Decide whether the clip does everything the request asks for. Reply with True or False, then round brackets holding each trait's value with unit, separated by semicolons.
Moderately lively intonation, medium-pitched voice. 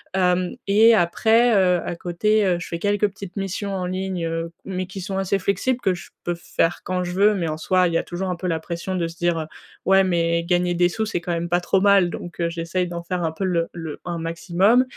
False (2.2 semitones; 180 Hz)